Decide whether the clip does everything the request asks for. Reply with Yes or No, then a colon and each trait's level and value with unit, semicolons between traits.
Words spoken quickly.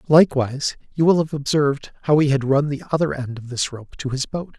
Yes: fast, 235 wpm